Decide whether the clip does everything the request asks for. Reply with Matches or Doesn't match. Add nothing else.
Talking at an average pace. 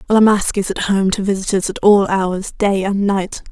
Doesn't match